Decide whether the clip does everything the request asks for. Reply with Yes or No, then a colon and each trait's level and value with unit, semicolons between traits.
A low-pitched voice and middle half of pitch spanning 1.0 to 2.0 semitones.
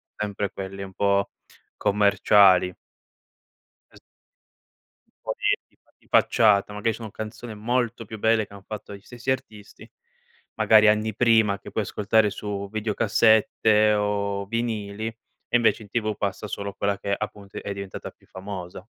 Yes: low, 105 Hz; narrow, 1.7 semitones